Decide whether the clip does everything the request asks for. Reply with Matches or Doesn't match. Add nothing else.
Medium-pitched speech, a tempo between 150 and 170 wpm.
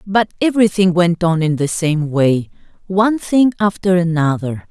Matches